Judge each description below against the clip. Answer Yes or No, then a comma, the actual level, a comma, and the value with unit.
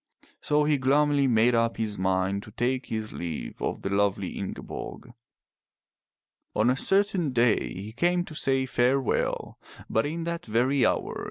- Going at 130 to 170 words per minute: Yes, average, 155 wpm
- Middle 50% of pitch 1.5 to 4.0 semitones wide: No, average, 5.3 semitones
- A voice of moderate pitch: No, low, 125 Hz